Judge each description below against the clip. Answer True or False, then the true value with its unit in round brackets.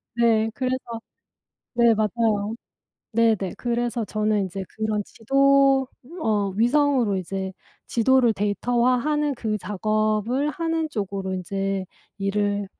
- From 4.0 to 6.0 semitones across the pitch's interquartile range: False (3.6 semitones)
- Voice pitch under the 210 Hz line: False (220 Hz)